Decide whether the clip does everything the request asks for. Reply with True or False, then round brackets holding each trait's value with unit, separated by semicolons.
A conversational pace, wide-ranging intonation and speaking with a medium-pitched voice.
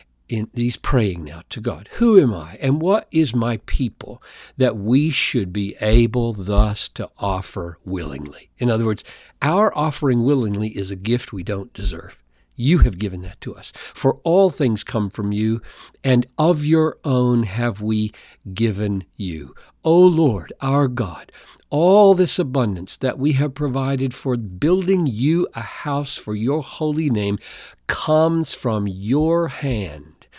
False (160 wpm; 6.3 semitones; 120 Hz)